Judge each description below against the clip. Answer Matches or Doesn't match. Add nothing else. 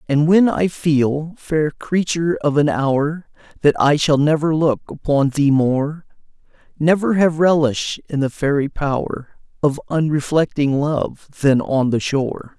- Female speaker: Doesn't match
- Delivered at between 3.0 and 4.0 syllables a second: Matches